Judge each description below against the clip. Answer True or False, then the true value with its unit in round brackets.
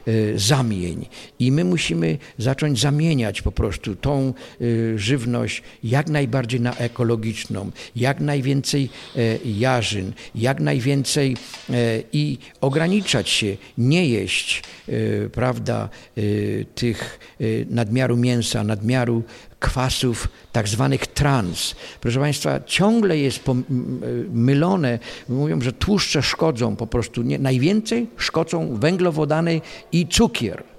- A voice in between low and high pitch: False (125 Hz)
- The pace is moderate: False (95 wpm)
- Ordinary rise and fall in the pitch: True (4.0 semitones)